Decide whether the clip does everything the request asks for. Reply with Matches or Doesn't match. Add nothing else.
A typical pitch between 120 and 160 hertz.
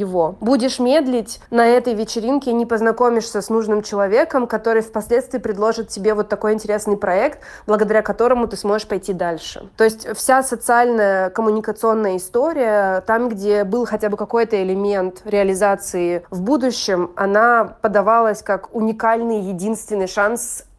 Doesn't match